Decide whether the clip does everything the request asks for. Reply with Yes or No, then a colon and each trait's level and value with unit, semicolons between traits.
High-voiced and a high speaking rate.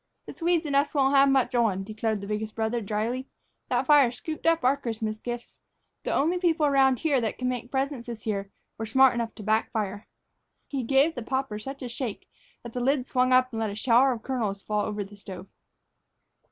Yes: high, 245 Hz; fast, 210 wpm